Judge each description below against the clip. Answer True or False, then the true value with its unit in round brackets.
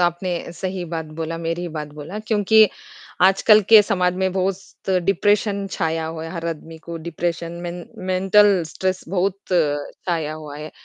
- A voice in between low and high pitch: True (175 Hz)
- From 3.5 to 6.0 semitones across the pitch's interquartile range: False (3.0 semitones)